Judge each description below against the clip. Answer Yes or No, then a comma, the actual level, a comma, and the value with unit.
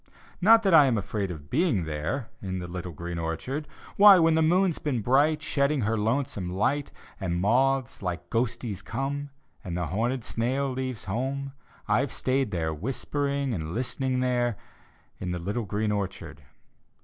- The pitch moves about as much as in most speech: No, wide, 6.8 semitones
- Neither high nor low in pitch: No, low, 120 Hz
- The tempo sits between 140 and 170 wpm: Yes, average, 160 wpm